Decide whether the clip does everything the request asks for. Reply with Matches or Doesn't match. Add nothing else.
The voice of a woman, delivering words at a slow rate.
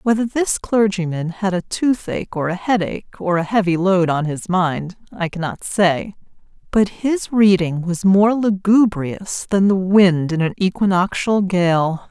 Doesn't match